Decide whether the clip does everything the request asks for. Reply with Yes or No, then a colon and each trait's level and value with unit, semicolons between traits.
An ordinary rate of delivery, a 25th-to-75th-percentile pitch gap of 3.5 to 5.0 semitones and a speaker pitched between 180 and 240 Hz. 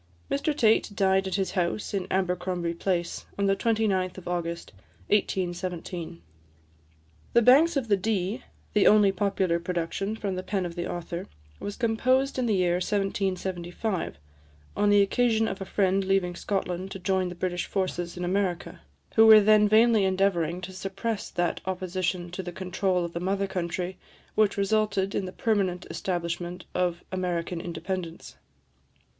No: average, 155 wpm; narrow, 2.5 semitones; high, 190 Hz